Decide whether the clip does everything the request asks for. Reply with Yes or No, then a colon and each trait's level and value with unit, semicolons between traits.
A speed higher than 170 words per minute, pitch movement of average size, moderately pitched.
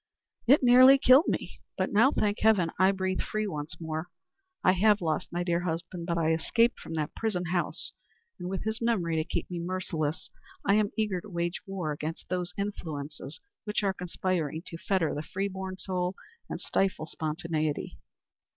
Yes: average, 180 wpm; average, 3.7 semitones; medium, 180 Hz